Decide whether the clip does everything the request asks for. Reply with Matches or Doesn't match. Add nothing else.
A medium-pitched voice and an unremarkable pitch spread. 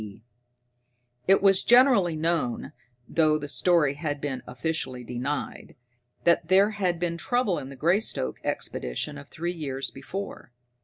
Matches